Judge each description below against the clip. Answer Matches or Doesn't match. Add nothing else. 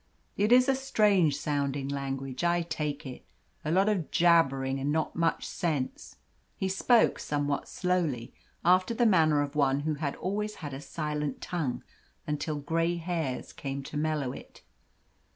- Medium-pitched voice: Matches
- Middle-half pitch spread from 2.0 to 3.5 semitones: Doesn't match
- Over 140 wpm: Matches